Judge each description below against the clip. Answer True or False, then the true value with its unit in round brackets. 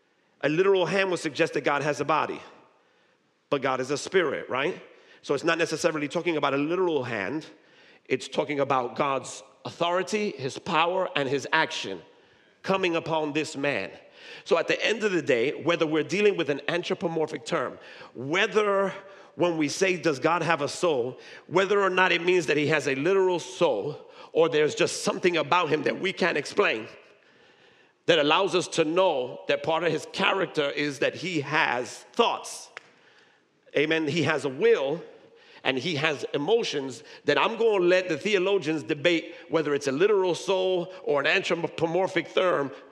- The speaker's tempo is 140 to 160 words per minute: False (170 wpm)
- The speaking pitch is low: False (180 Hz)